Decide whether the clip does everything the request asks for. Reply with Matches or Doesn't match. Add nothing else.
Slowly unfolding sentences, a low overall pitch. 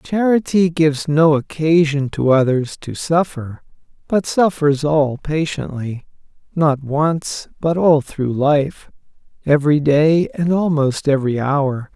Doesn't match